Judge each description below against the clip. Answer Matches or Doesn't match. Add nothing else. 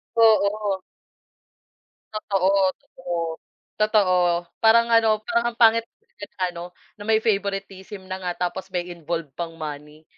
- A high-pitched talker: Matches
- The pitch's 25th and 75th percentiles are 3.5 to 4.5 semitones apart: Matches